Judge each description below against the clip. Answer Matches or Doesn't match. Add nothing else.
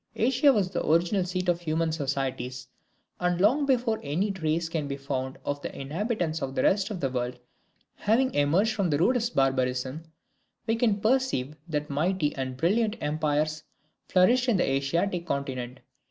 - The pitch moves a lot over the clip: Matches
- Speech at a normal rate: Matches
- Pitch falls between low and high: Matches